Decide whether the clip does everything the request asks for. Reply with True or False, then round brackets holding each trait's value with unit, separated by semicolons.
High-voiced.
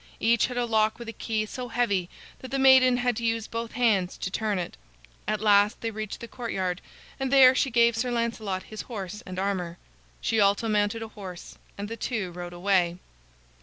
True (220 Hz)